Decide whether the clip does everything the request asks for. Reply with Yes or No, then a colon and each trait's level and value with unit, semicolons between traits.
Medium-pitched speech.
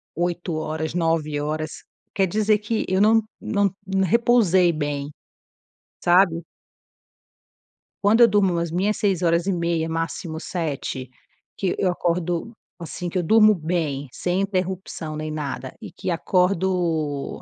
Yes: medium, 175 Hz